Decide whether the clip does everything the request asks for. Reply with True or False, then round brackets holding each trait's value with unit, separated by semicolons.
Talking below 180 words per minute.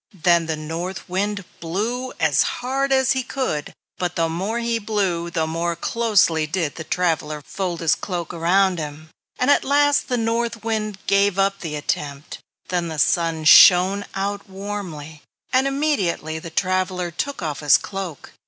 True (160 wpm)